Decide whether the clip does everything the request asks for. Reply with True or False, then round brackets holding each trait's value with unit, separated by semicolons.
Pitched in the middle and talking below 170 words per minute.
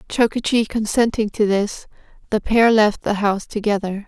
False (210 Hz; 145 wpm)